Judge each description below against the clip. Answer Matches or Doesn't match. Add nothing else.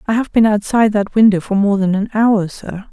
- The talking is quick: Matches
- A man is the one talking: Doesn't match